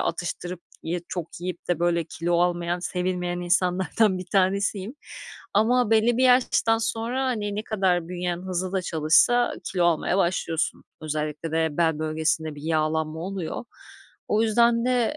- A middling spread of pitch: Yes, average, 4.2 semitones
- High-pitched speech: No, medium, 180 Hz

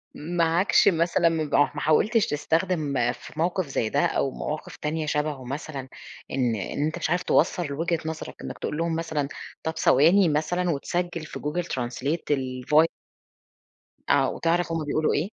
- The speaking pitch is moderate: Yes, medium, 155 Hz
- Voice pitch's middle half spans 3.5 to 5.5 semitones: No, average, 2.9 semitones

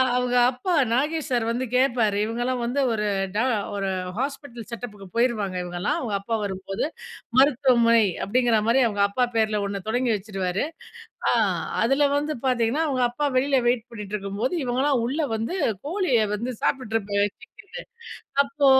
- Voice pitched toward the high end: Yes, high, 235 Hz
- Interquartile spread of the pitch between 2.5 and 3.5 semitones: No, average, 3.9 semitones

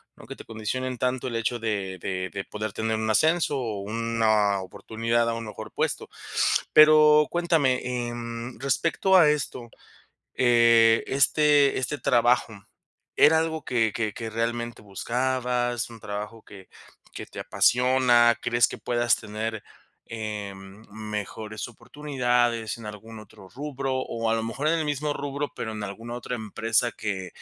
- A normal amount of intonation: Yes, average, 3.0 semitones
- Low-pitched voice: Yes, low, 115 Hz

